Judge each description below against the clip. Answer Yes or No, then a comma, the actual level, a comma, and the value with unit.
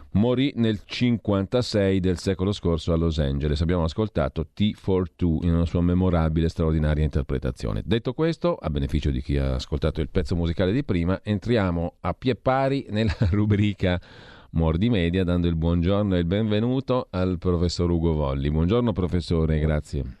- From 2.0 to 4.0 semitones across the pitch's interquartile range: No, average, 4.5 semitones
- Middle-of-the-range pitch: No, very low, 90 Hz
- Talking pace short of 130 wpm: No, average, 160 wpm